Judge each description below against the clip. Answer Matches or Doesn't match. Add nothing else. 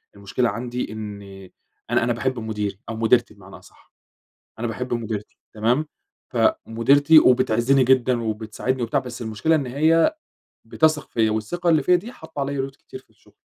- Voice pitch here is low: Matches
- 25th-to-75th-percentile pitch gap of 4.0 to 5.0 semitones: Matches